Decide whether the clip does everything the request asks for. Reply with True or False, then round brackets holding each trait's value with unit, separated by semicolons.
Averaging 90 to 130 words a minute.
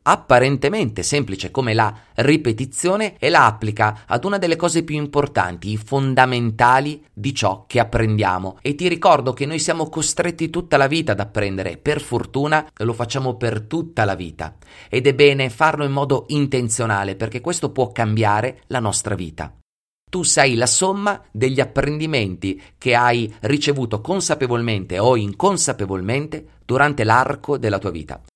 False (150 wpm)